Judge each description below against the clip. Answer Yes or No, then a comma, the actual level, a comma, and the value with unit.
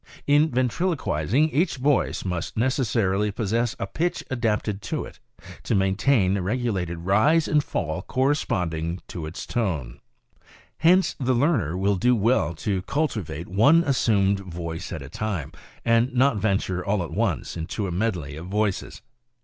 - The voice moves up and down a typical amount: No, wide, 6.2 semitones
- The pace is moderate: Yes, average, 150 wpm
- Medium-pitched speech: No, low, 105 Hz